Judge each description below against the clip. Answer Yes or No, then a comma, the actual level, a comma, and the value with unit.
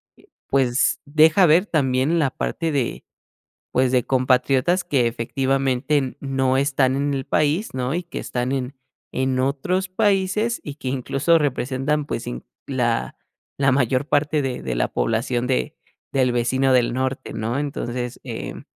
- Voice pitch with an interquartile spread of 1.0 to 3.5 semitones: Yes, narrow, 2.6 semitones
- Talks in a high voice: No, low, 135 Hz